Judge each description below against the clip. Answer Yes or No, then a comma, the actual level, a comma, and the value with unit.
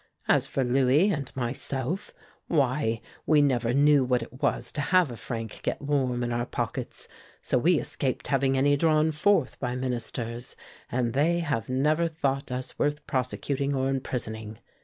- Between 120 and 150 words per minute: No, average, 160 wpm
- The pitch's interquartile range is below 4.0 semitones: Yes, average, 3.0 semitones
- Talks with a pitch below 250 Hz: Yes, low, 135 Hz